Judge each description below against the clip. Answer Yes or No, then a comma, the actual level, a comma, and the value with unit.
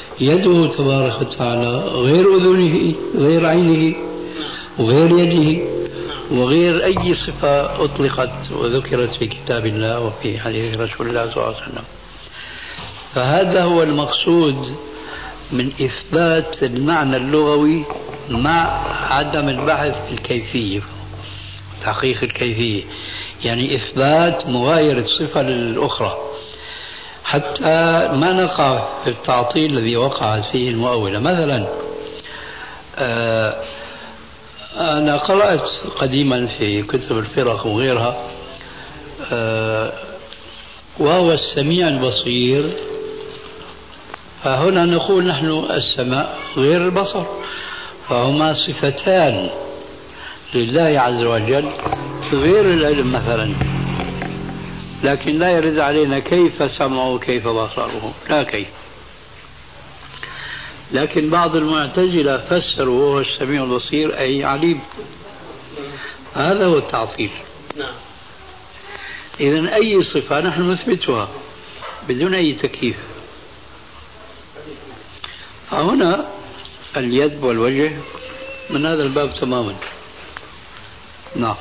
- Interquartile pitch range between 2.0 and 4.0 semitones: No, average, 5.1 semitones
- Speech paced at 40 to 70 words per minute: No, average, 85 wpm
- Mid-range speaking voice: Yes, medium, 145 Hz